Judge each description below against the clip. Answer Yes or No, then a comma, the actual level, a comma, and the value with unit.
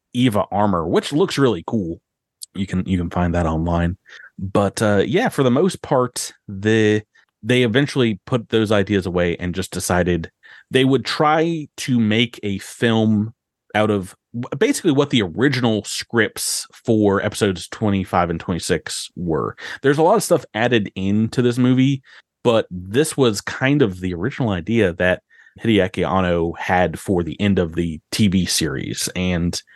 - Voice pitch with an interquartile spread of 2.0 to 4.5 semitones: No, average, 5.3 semitones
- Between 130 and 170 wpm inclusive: Yes, average, 160 wpm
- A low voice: Yes, low, 105 Hz